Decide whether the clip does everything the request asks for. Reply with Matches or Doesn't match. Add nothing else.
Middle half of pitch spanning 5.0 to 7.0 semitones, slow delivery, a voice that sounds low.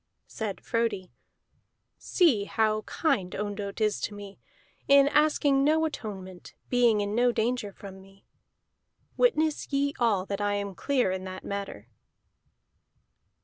Doesn't match